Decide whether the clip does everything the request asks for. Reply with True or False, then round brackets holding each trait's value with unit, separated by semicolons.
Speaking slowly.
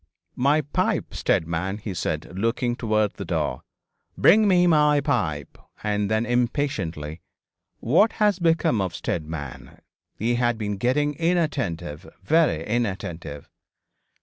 True (120 wpm)